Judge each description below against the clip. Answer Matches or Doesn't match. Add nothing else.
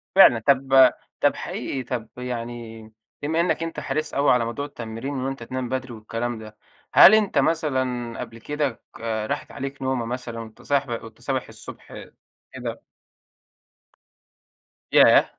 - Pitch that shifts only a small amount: Doesn't match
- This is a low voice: Matches